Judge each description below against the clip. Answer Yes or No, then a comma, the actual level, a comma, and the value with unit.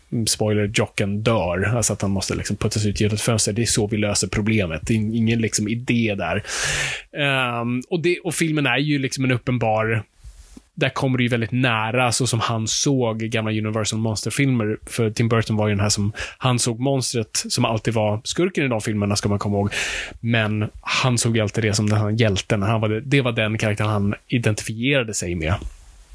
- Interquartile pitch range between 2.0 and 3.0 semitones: Yes, narrow, 2.5 semitones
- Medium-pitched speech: No, low, 110 Hz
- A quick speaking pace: Yes, fast, 205 wpm